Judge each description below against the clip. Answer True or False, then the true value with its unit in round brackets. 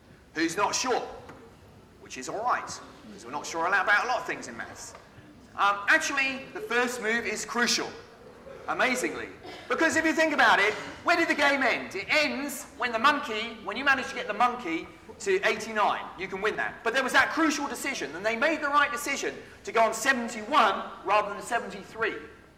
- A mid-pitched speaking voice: False (265 Hz)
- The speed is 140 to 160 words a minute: False (195 wpm)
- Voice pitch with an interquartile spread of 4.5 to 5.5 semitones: True (4.9 semitones)